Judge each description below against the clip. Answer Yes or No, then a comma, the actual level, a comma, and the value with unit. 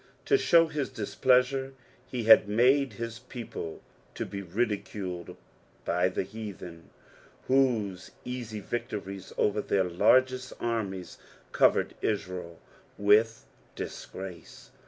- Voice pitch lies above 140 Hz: No, low, 110 Hz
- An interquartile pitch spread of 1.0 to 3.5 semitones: No, average, 4.7 semitones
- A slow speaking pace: Yes, slow, 105 wpm